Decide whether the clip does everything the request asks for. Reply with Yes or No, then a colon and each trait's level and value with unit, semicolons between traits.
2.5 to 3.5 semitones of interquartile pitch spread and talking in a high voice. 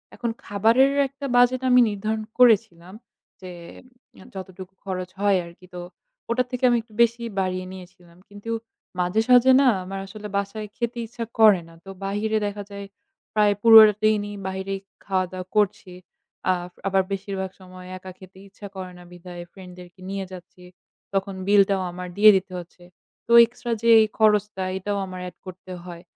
Yes: average, 2.9 semitones; high, 195 Hz